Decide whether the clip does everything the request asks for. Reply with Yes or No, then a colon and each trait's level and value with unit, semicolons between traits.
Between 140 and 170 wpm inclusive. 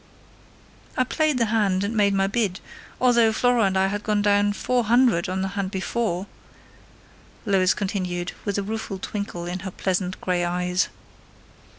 Yes: average, 160 wpm